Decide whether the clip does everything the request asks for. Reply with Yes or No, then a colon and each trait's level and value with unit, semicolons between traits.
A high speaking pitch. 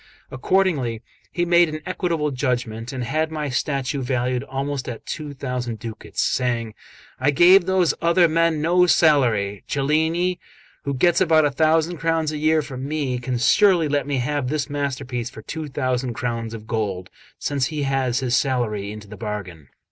No: medium, 140 Hz